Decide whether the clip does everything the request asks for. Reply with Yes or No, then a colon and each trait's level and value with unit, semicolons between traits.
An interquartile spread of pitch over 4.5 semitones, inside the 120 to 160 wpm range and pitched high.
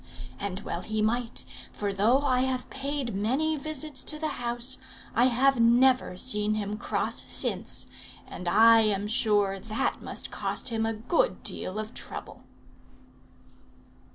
No: average, 3.8 semitones; average, 145 wpm; high, 230 Hz